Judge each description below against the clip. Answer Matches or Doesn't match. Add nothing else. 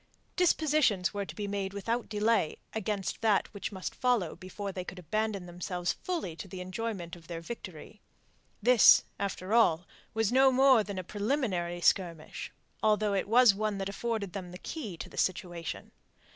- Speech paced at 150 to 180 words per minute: Matches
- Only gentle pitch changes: Doesn't match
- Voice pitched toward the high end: Matches